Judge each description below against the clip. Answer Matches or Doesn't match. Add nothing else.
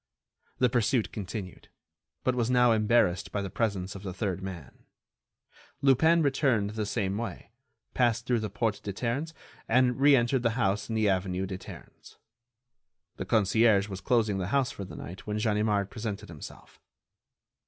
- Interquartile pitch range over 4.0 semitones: Doesn't match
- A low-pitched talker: Matches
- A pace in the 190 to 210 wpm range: Doesn't match